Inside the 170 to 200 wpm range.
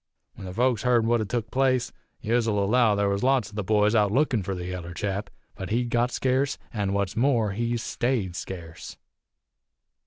Yes: average, 190 wpm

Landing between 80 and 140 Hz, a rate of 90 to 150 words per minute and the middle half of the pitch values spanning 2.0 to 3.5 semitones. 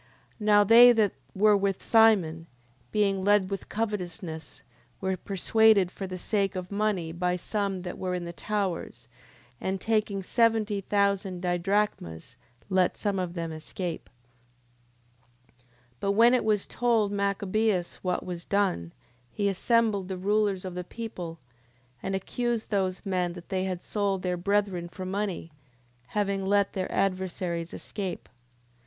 No: high, 195 Hz; average, 145 wpm; narrow, 2.5 semitones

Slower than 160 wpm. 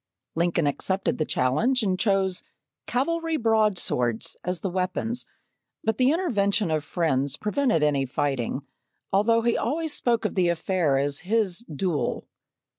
Yes: slow, 135 wpm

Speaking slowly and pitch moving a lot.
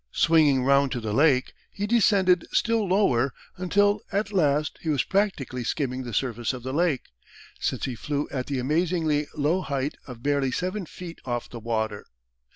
No: average, 170 wpm; wide, 6.0 semitones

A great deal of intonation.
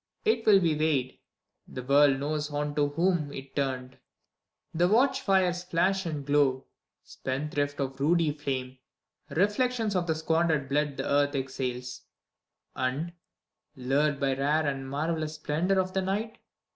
No: average, 4.2 semitones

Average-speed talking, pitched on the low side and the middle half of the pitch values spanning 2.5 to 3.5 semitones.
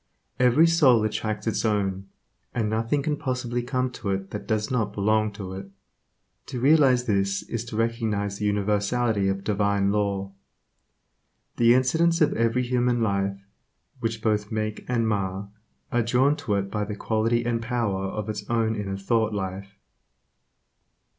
Yes: average, 155 wpm; low, 110 Hz; average, 3.2 semitones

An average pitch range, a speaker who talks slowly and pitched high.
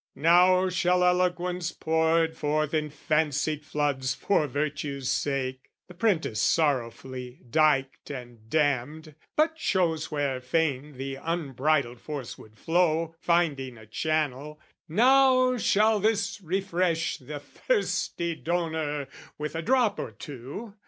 No: average, 4.3 semitones; slow, 120 wpm; medium, 155 Hz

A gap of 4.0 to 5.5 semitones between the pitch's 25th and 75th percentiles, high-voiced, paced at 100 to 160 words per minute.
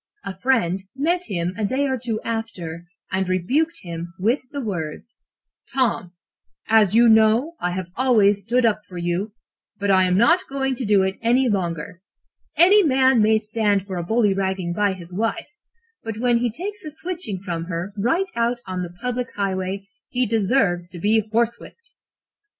No: average, 5.0 semitones; high, 215 Hz; average, 175 wpm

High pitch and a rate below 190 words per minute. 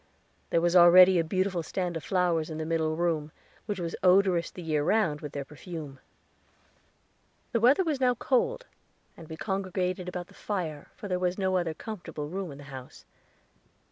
No: medium, 175 Hz; average, 180 wpm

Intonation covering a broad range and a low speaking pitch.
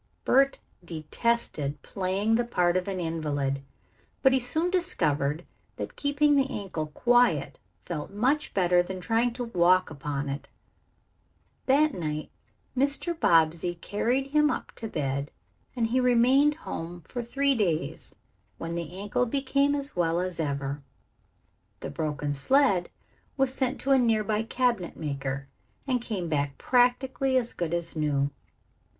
No: wide, 8.4 semitones; high, 195 Hz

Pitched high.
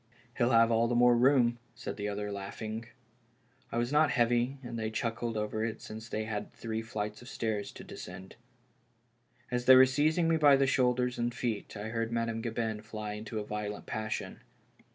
No: low, 115 Hz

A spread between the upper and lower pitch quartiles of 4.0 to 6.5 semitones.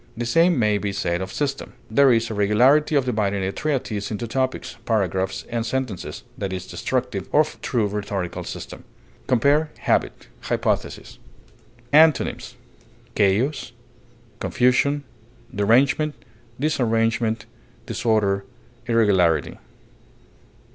Yes: average, 4.5 semitones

